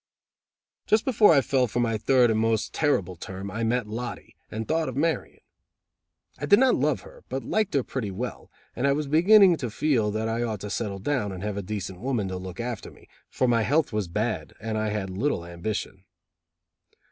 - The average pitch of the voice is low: Yes, low, 115 Hz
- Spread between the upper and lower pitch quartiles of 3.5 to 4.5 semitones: No, average, 5.1 semitones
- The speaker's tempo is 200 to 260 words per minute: Yes, fast, 205 wpm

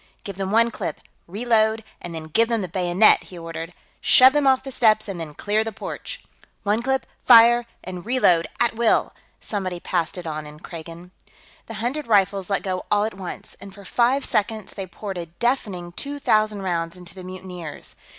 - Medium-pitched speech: No, high, 200 Hz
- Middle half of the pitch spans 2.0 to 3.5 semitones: No, average, 4.5 semitones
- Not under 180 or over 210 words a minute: Yes, average, 190 wpm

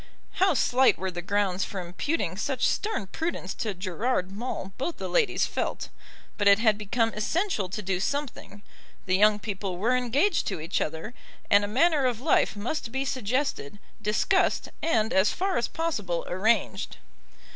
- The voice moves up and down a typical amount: No, wide, 5.7 semitones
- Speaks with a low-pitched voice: No, high, 215 Hz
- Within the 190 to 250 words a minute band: No, average, 165 wpm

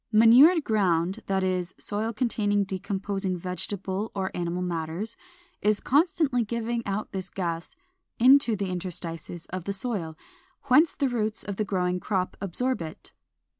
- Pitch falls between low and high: No, high, 200 Hz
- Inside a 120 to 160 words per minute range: Yes, average, 140 wpm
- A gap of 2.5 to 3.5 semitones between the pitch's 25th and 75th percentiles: No, average, 3.9 semitones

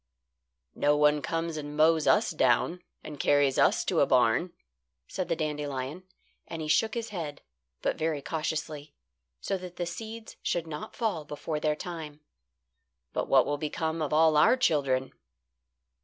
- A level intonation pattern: Yes, narrow, 2.3 semitones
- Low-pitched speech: No, medium, 155 Hz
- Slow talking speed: No, average, 155 wpm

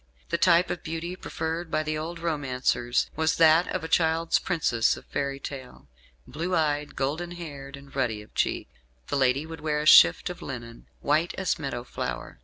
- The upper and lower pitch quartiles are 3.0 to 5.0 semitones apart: Yes, average, 3.5 semitones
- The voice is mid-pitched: Yes, medium, 155 Hz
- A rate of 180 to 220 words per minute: Yes, average, 185 wpm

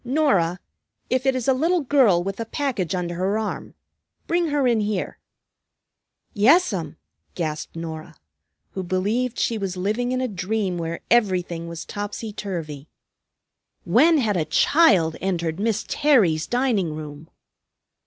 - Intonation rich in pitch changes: Yes, wide, 6.6 semitones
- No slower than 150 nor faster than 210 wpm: No, average, 140 wpm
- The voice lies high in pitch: Yes, high, 200 Hz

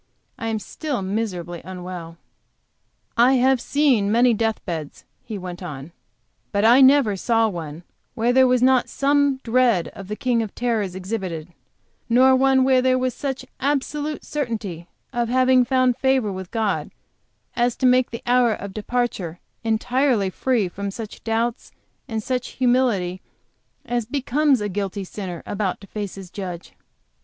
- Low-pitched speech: No, high, 230 Hz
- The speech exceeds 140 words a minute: Yes, average, 155 wpm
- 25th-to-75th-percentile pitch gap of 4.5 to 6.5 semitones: Yes, average, 4.8 semitones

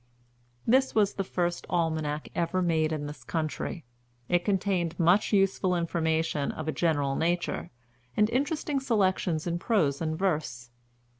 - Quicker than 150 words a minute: No, average, 140 wpm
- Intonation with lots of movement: No, average, 3.6 semitones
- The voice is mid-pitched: Yes, medium, 170 Hz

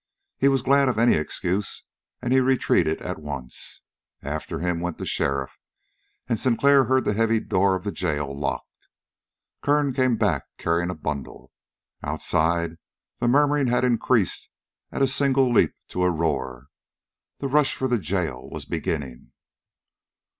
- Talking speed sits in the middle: Yes, average, 150 wpm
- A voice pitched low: Yes, low, 100 Hz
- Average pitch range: No, wide, 8.6 semitones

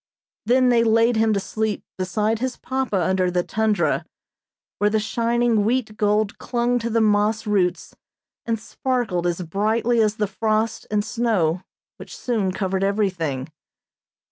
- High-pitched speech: Yes, high, 215 Hz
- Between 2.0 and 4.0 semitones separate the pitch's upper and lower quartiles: Yes, average, 2.9 semitones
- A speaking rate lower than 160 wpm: Yes, average, 145 wpm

